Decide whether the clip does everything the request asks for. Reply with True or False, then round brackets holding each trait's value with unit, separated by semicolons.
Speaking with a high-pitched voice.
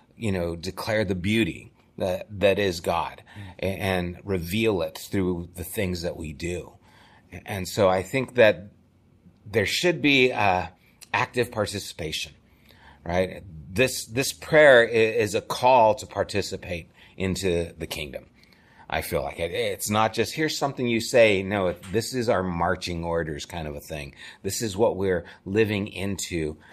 False (95 Hz)